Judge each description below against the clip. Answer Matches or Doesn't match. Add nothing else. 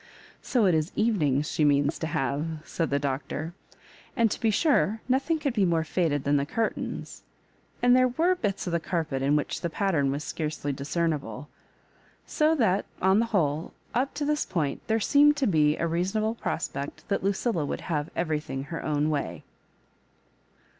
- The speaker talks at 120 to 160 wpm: Doesn't match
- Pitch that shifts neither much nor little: Doesn't match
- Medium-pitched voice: Matches